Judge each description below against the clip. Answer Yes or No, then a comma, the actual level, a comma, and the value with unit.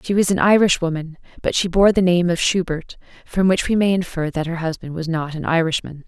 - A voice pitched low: No, medium, 175 Hz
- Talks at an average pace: No, fast, 225 wpm